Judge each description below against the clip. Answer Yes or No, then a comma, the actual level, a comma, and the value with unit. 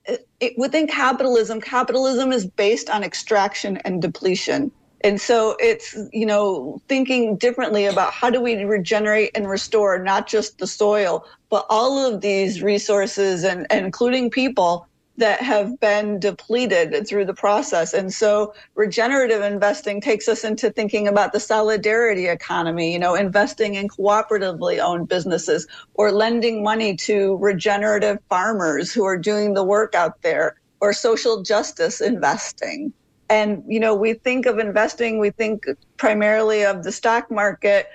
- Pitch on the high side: Yes, high, 215 Hz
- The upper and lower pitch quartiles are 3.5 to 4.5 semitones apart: No, narrow, 2.4 semitones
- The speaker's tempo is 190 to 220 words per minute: No, average, 150 wpm